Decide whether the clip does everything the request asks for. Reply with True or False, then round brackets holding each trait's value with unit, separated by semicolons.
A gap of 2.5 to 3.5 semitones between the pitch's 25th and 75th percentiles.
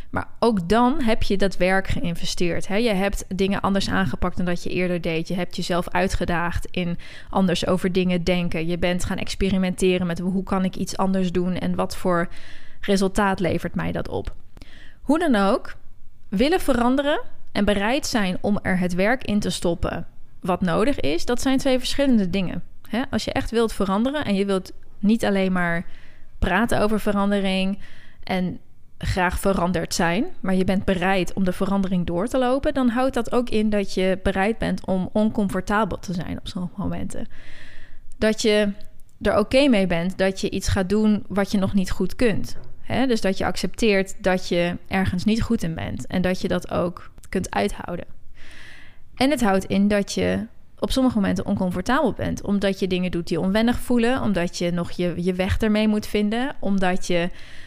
True (3.1 semitones)